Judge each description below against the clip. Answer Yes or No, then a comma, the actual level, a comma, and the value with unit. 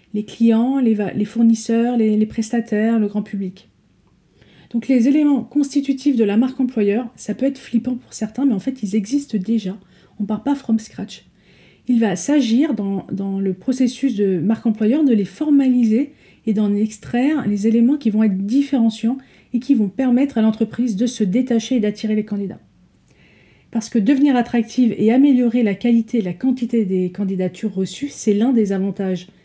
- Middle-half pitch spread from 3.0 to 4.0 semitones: Yes, average, 3.3 semitones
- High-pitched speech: Yes, high, 230 Hz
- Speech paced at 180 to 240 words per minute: Yes, average, 185 wpm